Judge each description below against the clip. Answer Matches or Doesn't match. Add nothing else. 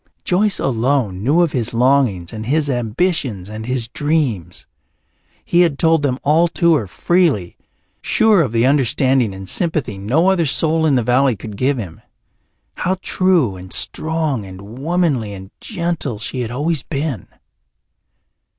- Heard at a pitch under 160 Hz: Matches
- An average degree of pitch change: Doesn't match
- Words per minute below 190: Matches